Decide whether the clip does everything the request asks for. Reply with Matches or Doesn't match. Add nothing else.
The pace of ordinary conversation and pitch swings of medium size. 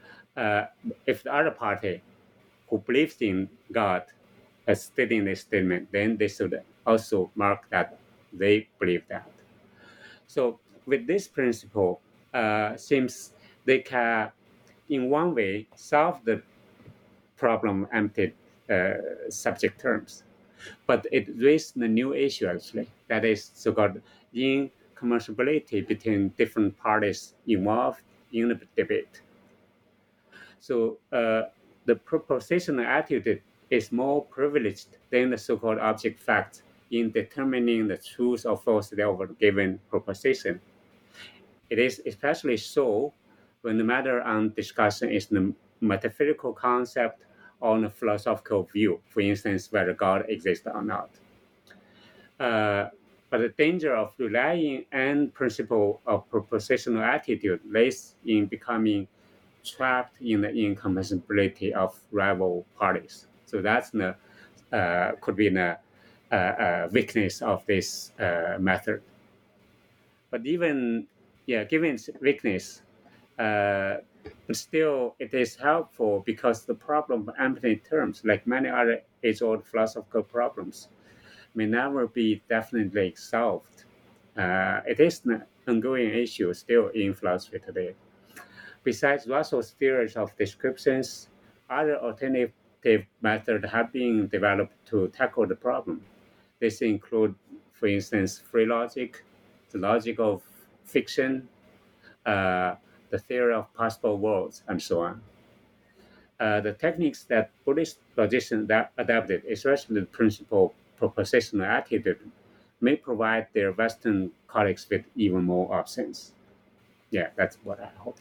Doesn't match